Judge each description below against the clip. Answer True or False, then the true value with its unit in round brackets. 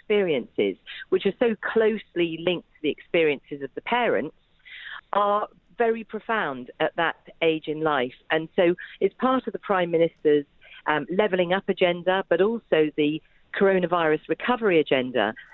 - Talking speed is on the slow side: False (145 wpm)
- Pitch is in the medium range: True (180 Hz)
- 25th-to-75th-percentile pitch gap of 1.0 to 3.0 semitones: False (5.5 semitones)